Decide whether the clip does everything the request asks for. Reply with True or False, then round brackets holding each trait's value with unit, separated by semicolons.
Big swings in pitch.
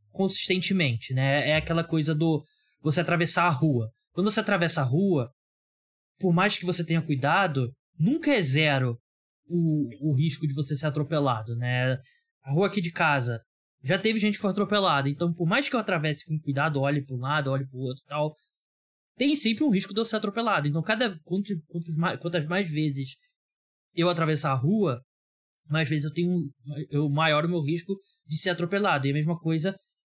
False (4.7 semitones)